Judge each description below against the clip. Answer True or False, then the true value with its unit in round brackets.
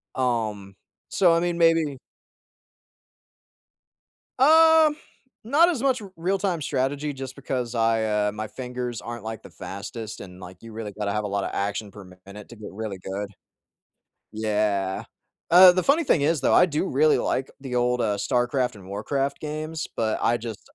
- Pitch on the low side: True (120 Hz)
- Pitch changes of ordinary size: False (6.8 semitones)